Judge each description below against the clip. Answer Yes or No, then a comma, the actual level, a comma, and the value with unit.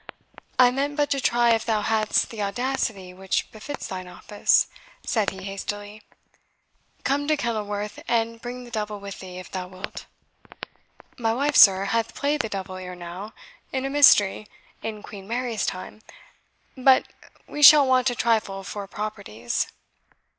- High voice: Yes, high, 215 Hz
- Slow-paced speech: No, average, 155 wpm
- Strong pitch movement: No, average, 4.2 semitones